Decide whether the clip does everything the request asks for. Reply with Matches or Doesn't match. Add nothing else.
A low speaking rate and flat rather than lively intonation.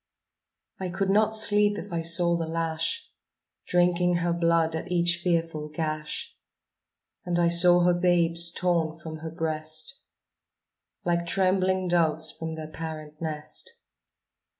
Matches